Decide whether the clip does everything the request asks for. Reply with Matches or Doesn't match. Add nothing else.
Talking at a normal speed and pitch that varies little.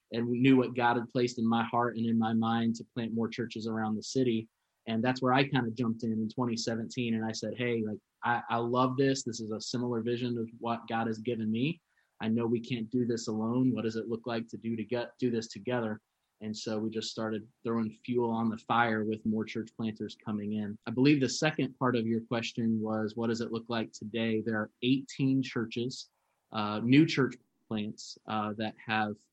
Doesn't match